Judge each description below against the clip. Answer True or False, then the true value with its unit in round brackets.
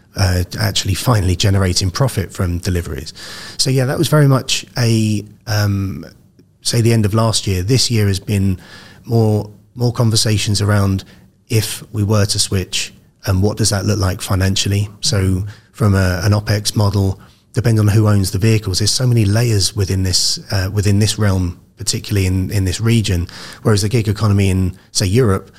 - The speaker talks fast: True (175 wpm)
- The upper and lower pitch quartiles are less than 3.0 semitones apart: True (2.5 semitones)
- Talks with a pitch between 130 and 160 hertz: False (105 Hz)